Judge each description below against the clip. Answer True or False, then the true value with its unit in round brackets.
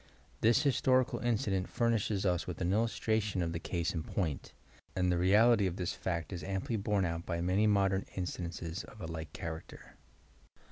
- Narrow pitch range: False (3.8 semitones)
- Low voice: True (95 Hz)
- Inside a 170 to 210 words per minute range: True (175 wpm)